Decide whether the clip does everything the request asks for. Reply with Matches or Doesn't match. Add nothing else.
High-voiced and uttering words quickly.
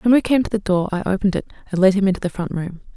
Matches